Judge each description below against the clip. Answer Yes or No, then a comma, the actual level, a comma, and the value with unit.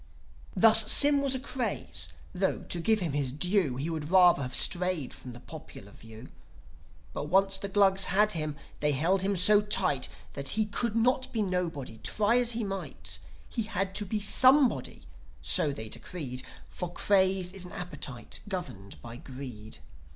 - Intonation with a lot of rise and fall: Yes, wide, 6.7 semitones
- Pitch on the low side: No, medium, 180 Hz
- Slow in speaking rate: No, average, 170 wpm